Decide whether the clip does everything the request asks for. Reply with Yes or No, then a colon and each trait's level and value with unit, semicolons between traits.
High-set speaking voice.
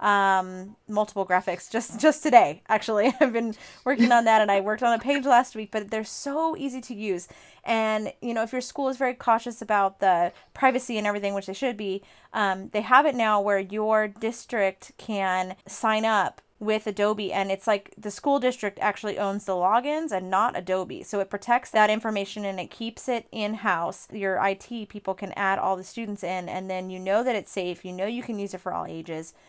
Yes: high, 210 Hz